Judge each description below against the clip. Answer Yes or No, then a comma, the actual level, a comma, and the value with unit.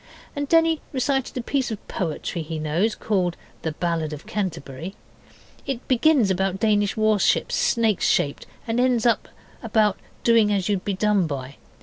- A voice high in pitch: Yes, high, 205 Hz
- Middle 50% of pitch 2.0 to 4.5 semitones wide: No, average, 5.1 semitones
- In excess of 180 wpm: No, average, 150 wpm